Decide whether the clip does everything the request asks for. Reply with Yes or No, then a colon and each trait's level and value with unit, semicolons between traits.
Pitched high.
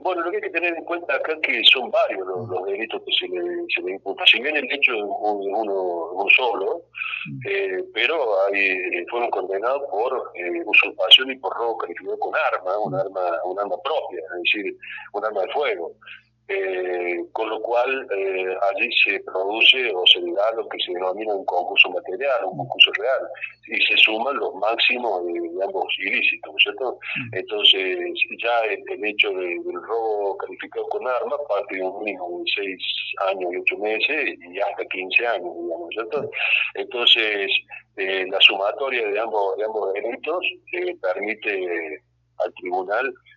Yes: very high, 370 Hz